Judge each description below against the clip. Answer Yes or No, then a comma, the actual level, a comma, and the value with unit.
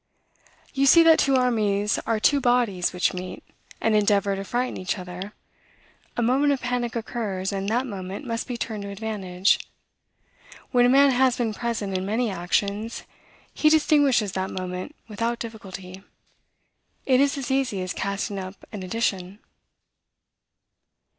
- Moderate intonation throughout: Yes, average, 4.4 semitones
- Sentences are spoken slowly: No, average, 150 wpm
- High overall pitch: Yes, high, 215 Hz